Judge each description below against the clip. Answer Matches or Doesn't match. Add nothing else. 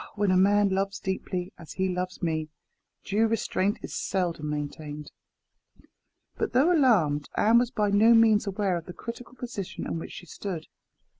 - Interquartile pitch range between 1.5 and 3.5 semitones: Doesn't match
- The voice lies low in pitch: Doesn't match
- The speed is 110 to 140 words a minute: Doesn't match